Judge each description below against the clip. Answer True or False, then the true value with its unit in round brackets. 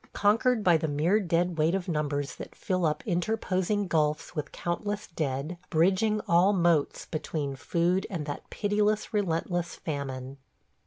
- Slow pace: False (145 wpm)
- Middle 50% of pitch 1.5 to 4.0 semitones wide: False (4.5 semitones)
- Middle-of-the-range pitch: True (170 Hz)